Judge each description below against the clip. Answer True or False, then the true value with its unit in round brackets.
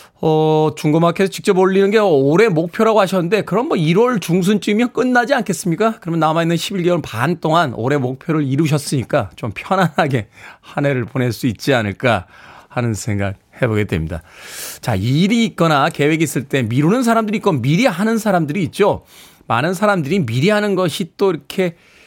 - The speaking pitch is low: False (165 Hz)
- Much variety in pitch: True (6.4 semitones)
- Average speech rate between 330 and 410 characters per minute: True (365 characters per minute)